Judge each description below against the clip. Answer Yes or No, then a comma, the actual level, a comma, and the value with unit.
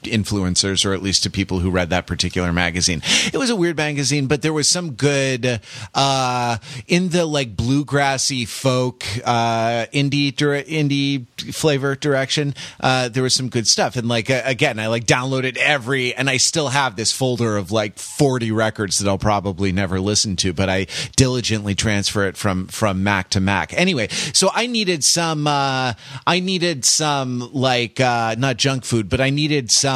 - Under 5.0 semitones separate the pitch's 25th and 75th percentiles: No, average, 5.3 semitones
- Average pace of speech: Yes, average, 180 wpm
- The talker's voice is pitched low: Yes, low, 130 Hz